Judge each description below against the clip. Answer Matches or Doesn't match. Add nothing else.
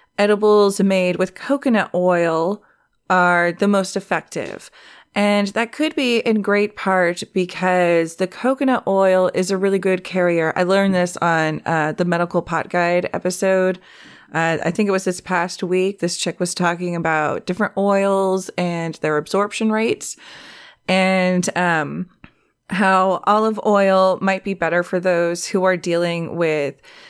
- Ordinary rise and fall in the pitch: Doesn't match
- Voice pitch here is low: Doesn't match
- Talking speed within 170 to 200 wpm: Doesn't match